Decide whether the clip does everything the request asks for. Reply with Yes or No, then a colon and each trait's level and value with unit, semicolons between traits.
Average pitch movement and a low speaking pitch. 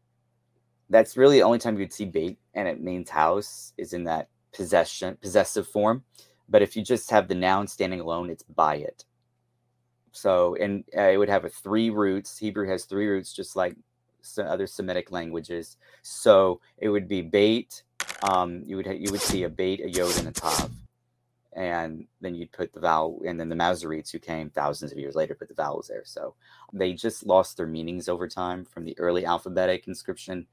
Yes: average, 3.9 semitones; very low, 95 Hz